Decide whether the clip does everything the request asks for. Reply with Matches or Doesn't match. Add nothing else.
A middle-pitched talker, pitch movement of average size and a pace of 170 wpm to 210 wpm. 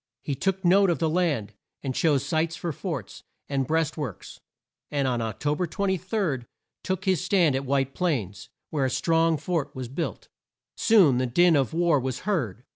Matches